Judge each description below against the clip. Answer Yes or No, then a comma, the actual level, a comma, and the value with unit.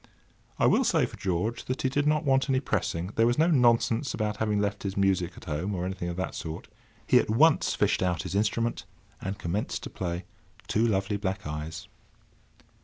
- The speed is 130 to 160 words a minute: No, average, 200 wpm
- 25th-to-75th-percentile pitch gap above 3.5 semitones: Yes, average, 4.5 semitones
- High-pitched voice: No, low, 100 Hz